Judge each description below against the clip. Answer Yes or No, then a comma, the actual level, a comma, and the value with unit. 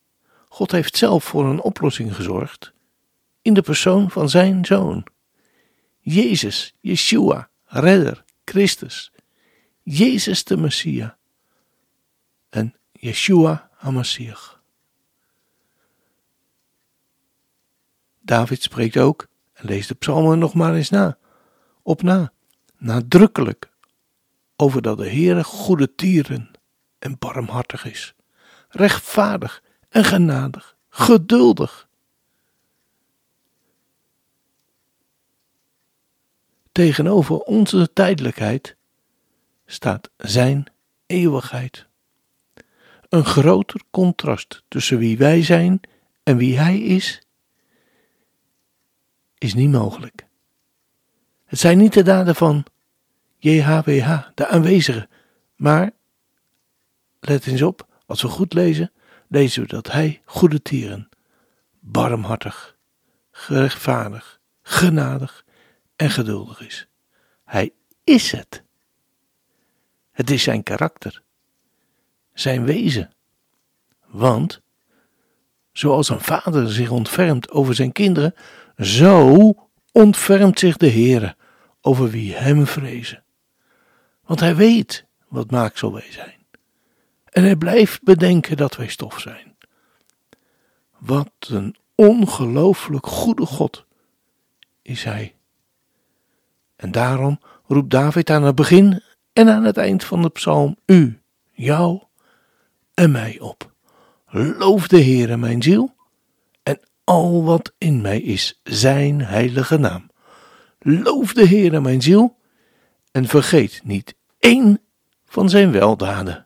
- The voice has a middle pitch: Yes, medium, 150 Hz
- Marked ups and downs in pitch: Yes, wide, 6.7 semitones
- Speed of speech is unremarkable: No, slow, 100 wpm